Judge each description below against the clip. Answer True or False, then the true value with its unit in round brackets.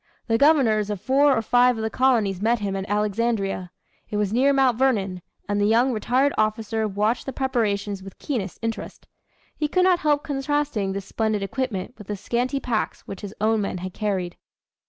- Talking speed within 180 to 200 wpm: True (190 wpm)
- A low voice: False (220 Hz)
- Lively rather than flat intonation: False (4.3 semitones)